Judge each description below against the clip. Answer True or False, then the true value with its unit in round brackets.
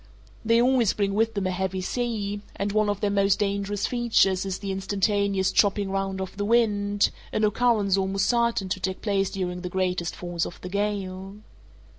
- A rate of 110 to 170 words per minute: False (185 wpm)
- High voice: True (200 Hz)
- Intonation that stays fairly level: True (1.7 semitones)